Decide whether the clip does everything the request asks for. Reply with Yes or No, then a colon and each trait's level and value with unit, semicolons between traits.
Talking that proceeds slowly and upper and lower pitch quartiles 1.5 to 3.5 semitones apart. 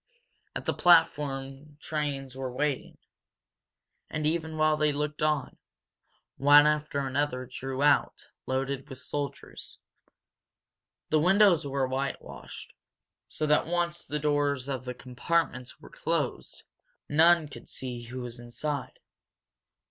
Yes: slow, 120 wpm; narrow, 2.5 semitones